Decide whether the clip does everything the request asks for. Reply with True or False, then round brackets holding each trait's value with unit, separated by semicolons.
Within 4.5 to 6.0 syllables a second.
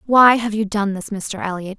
True (4.9 syllables/s)